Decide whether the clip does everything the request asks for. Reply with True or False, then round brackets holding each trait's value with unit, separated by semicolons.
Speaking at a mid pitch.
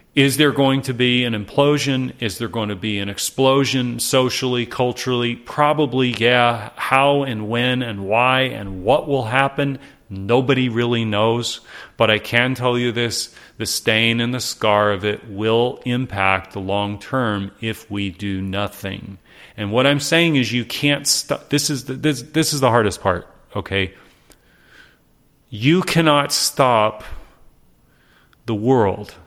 False (120 Hz)